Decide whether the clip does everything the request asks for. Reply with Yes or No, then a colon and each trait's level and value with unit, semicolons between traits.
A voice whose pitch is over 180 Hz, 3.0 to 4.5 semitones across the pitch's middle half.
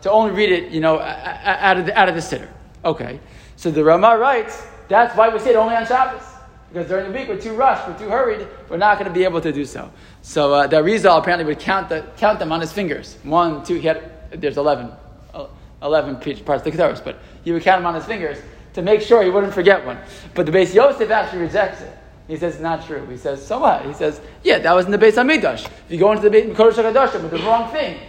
No: high, 190 Hz; wide, 5.4 semitones